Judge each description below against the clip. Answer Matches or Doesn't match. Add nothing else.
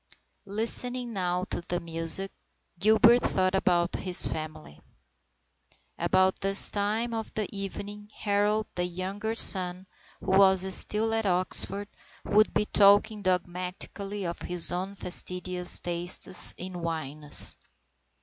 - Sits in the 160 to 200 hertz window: Matches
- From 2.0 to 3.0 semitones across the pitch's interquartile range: Matches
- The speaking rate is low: Matches